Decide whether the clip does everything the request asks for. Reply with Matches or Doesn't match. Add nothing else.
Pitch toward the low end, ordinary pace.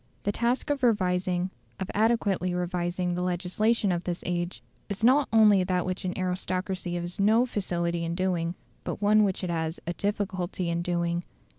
Doesn't match